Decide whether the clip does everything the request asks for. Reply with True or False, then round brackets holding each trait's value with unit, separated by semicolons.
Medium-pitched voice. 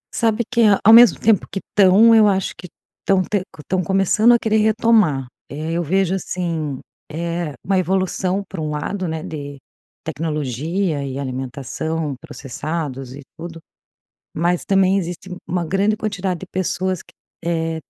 True (175 Hz)